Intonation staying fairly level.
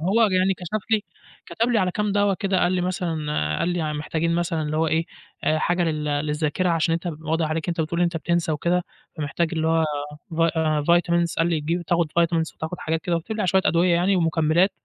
Yes: narrow, 2.1 semitones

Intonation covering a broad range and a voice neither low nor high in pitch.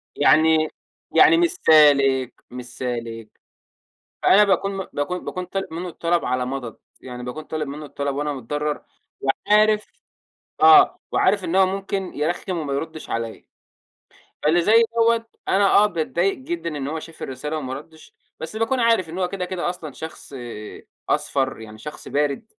Yes: wide, 5.7 semitones; medium, 160 Hz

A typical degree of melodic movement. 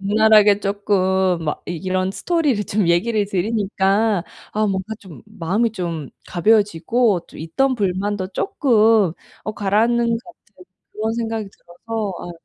Yes: average, 3.1 semitones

